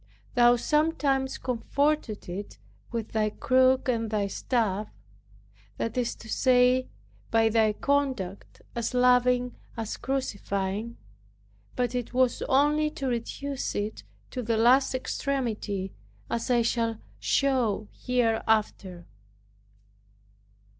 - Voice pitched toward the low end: No, high, 240 Hz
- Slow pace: Yes, slow, 105 wpm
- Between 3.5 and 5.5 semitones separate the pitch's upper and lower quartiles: No, average, 2.9 semitones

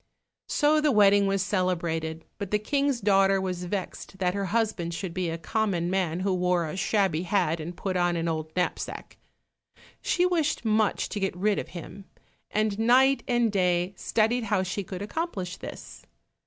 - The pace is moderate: Yes, average, 175 wpm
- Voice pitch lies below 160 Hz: No, high, 195 Hz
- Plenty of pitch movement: No, average, 3.2 semitones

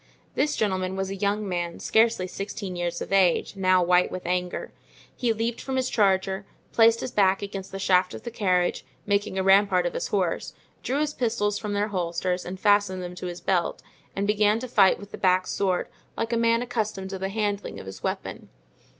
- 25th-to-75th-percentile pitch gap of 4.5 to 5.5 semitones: No, narrow, 2.5 semitones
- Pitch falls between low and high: No, high, 195 Hz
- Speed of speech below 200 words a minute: No, fast, 205 wpm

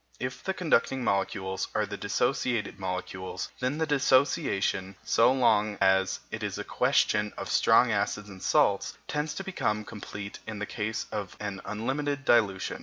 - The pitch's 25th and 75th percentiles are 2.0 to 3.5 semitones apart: No, average, 5.0 semitones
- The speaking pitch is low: Yes, low, 105 Hz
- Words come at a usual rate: Yes, average, 160 wpm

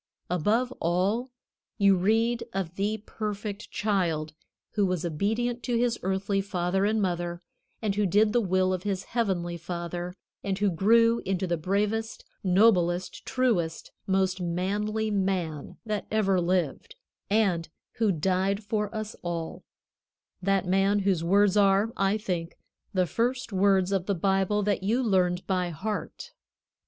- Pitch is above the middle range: Yes, high, 195 Hz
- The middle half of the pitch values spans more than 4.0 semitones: No, average, 2.8 semitones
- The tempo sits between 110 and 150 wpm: Yes, average, 145 wpm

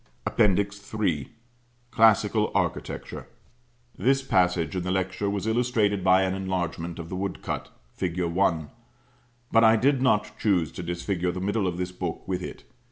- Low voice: Yes, very low, 95 Hz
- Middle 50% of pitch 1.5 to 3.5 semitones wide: Yes, average, 2.9 semitones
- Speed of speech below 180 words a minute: Yes, average, 160 wpm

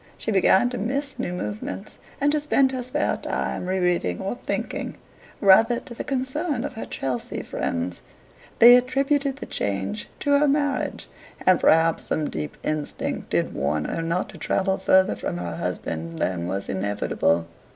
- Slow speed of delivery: No, average, 165 wpm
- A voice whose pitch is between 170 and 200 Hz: Yes, high, 190 Hz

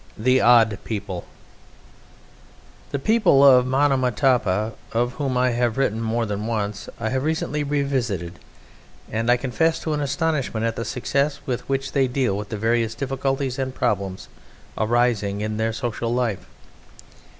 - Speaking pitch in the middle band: No, low, 120 Hz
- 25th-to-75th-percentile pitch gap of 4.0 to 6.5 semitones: No, average, 3.5 semitones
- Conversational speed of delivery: Yes, average, 150 wpm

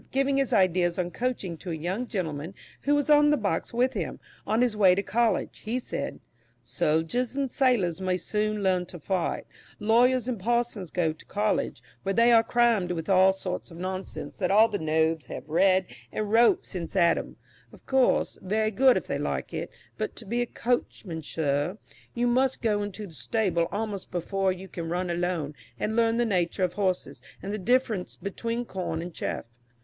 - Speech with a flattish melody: No, average, 4.9 semitones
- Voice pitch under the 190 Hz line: No, high, 195 Hz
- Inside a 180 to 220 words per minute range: Yes, average, 190 wpm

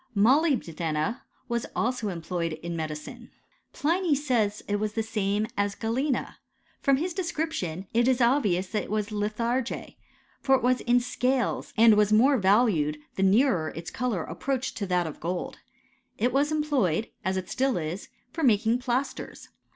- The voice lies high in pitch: Yes, high, 225 Hz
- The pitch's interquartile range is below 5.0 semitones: No, wide, 5.5 semitones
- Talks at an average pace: Yes, average, 170 wpm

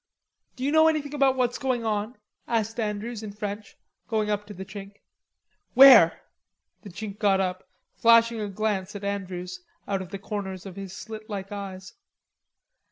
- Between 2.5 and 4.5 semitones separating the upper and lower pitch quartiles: Yes, average, 2.9 semitones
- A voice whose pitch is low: No, high, 210 Hz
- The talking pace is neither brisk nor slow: Yes, average, 165 wpm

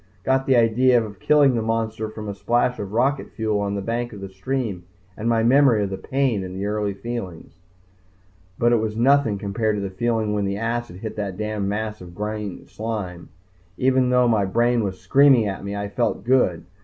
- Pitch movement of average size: Yes, average, 3.0 semitones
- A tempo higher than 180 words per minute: Yes, fast, 205 wpm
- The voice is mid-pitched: No, low, 110 Hz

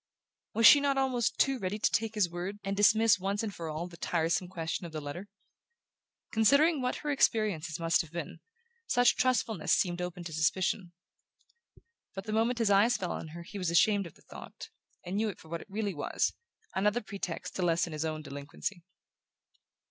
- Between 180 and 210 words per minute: Yes, average, 190 wpm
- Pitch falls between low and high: No, high, 195 Hz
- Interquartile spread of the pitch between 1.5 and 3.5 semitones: No, average, 4.7 semitones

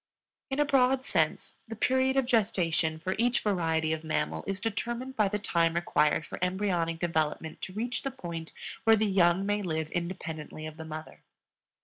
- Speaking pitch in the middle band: Yes, medium, 180 Hz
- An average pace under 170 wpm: No, average, 175 wpm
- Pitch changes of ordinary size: No, wide, 5.9 semitones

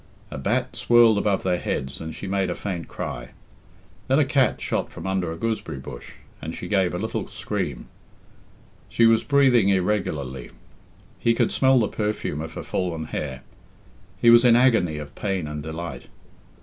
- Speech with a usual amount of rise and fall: No, wide, 6.3 semitones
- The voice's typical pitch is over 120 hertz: No, very low, 95 Hz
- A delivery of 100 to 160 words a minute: No, average, 175 wpm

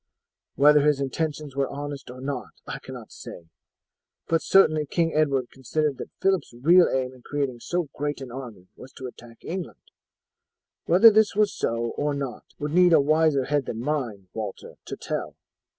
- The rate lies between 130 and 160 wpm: No, average, 170 wpm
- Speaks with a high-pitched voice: No, medium, 145 Hz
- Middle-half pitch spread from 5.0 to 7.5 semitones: No, average, 3.5 semitones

